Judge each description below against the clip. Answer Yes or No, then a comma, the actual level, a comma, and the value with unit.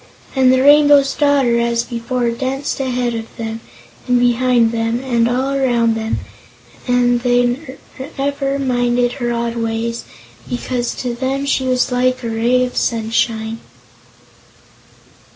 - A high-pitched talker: Yes, high, 245 Hz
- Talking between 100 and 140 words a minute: Yes, slow, 135 wpm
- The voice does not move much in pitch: Yes, narrow, 1.9 semitones